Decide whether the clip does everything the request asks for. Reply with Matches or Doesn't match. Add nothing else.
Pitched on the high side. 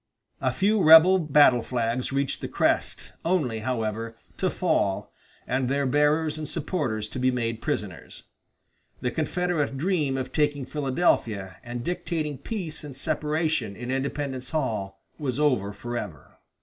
Doesn't match